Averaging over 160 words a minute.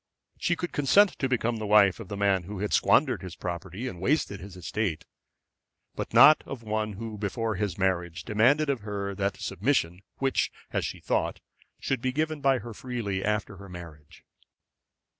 Yes: average, 180 wpm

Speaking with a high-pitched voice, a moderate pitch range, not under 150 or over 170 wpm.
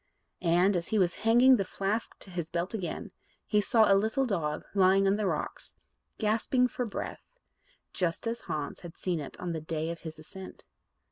No: high, 195 Hz; average, 4.4 semitones; average, 190 wpm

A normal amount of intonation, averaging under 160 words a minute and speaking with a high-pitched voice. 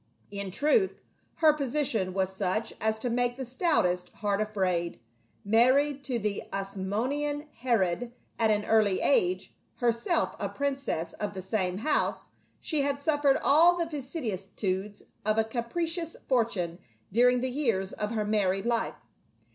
No: wide, 6.1 semitones; average, 145 wpm; high, 225 Hz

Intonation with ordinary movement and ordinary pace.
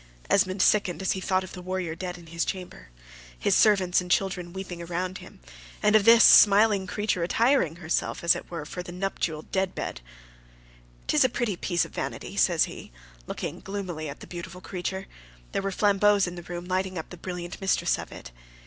No: narrow, 2.0 semitones; average, 195 wpm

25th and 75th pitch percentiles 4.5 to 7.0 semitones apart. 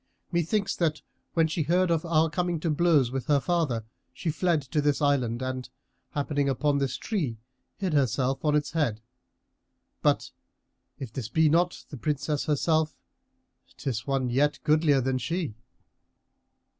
No: average, 3.6 semitones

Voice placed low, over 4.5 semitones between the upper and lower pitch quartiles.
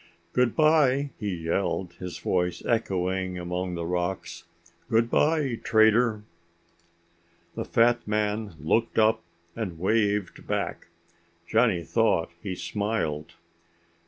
No: low, 105 Hz; average, 4.2 semitones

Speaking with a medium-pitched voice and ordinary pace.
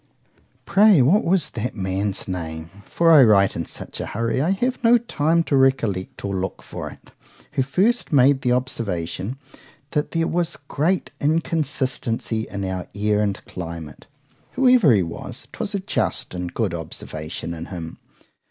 No: low, 120 Hz; average, 150 wpm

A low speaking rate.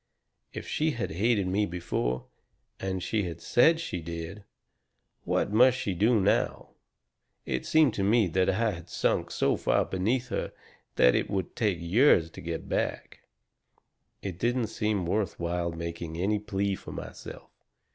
No: average, 155 wpm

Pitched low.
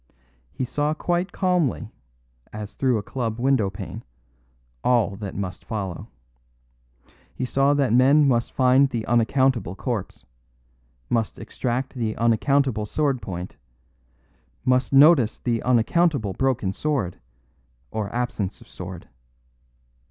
Yes: low, 120 Hz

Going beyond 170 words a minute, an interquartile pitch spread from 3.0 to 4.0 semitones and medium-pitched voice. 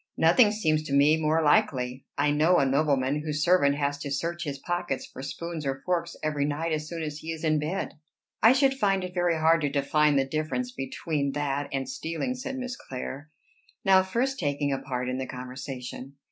Yes: average, 200 wpm; average, 3.6 semitones; medium, 155 Hz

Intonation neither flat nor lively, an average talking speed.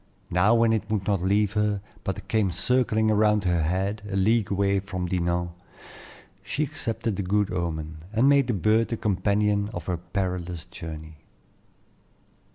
Yes: average, 3.3 semitones; average, 160 wpm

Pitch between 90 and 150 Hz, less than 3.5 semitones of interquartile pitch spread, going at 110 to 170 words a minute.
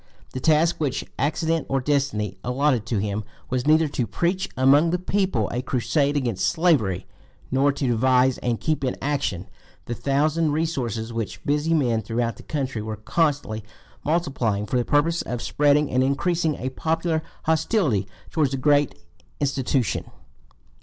No: low, 135 Hz; average, 4.7 semitones; average, 155 wpm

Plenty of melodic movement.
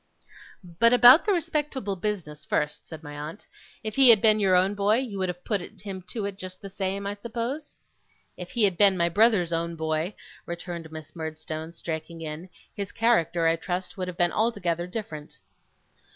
No: average, 4.3 semitones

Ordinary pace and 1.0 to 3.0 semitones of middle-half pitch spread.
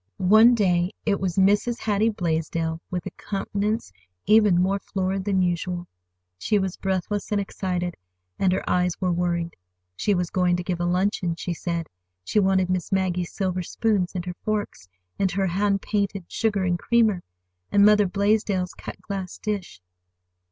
Yes: average, 165 wpm; narrow, 2.5 semitones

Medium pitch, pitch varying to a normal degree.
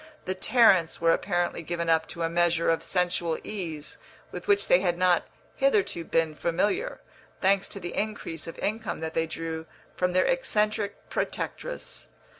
Yes: medium, 175 Hz; average, 3.6 semitones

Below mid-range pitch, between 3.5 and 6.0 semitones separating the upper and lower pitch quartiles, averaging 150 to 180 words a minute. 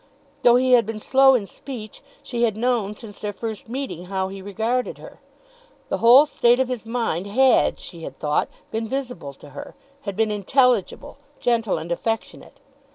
No: high, 225 Hz; average, 3.9 semitones; average, 175 wpm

